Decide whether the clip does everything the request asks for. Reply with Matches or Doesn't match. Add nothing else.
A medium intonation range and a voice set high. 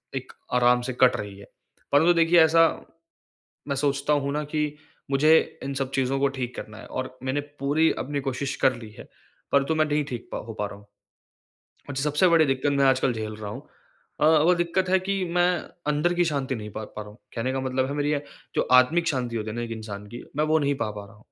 Doesn't match